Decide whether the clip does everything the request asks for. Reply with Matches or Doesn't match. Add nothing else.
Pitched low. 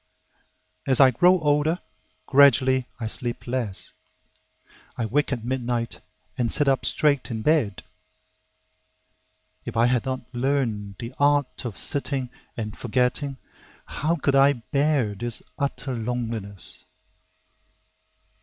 Matches